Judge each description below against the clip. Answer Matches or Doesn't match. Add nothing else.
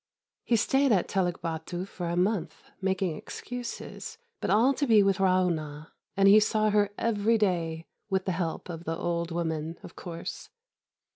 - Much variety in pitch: Doesn't match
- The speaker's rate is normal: Matches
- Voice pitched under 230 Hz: Matches